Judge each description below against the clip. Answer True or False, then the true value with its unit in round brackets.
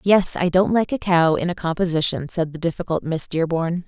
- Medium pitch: True (170 Hz)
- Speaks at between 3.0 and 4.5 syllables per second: False (5.4 syllables/s)